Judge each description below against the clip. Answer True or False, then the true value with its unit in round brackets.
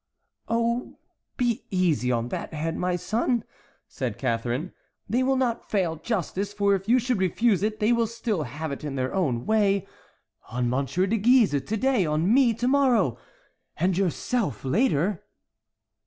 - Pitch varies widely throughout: True (7.4 semitones)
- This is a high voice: True (195 Hz)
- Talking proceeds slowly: False (160 wpm)